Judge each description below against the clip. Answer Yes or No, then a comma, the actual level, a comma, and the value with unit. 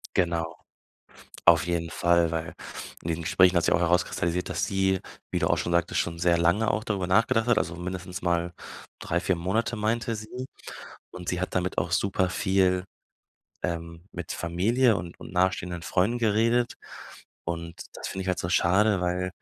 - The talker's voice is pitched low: Yes, very low, 90 Hz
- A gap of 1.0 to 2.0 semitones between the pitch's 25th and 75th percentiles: No, narrow, 2.4 semitones